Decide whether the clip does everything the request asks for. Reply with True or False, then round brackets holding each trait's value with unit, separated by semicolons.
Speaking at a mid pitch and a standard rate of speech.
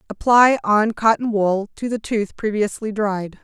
False (215 Hz; 155 wpm)